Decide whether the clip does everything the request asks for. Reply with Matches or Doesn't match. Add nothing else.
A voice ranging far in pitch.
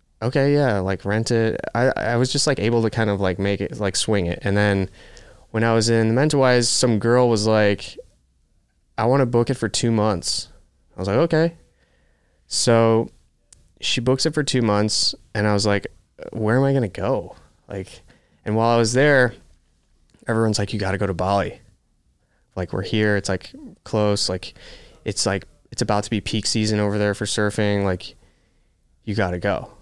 Doesn't match